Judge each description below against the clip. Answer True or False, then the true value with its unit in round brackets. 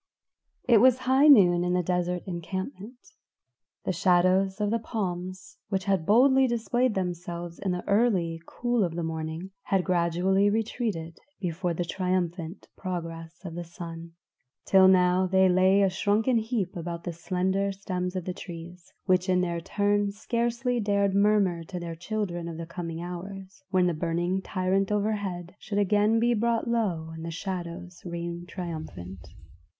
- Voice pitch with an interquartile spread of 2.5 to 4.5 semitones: True (2.9 semitones)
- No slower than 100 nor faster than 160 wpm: True (155 wpm)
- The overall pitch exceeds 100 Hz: True (185 Hz)